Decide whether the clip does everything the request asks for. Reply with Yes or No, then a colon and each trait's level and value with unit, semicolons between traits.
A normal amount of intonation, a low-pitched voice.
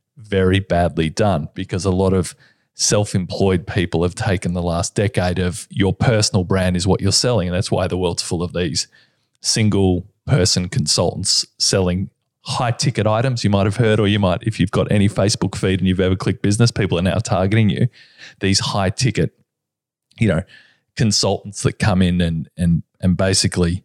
Yes: average, 3.1 semitones; very low, 95 Hz